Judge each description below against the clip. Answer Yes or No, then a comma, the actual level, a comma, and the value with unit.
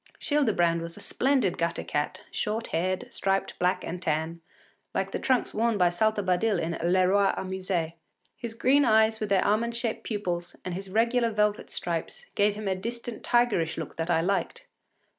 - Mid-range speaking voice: No, high, 195 Hz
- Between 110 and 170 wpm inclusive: No, average, 180 wpm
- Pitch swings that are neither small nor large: Yes, average, 4.5 semitones